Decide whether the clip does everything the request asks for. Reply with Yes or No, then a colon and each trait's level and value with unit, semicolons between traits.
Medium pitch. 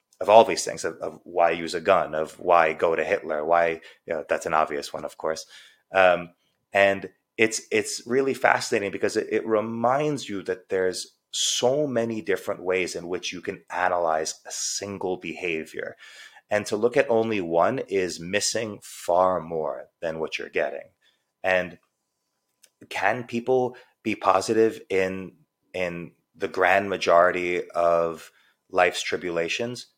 No: very low, 95 Hz